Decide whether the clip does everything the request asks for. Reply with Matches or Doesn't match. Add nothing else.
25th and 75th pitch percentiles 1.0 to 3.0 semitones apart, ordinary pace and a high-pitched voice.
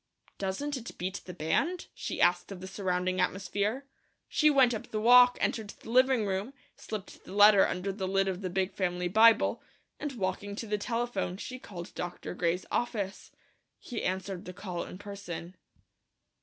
Doesn't match